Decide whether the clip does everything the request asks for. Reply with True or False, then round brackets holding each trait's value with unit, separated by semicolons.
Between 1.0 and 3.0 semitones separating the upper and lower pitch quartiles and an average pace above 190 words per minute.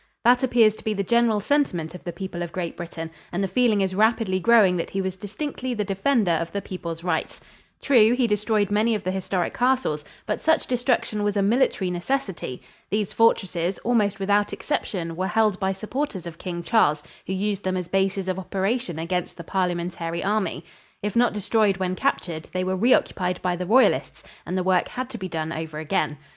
False (3.8 semitones; 200 wpm)